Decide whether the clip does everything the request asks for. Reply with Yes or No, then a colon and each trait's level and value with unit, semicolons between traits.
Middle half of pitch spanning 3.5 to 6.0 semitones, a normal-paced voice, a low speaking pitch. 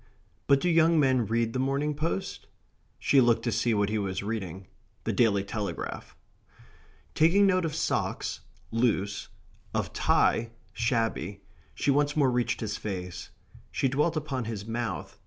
Yes: wide, 5.6 semitones; average, 150 wpm; low, 120 Hz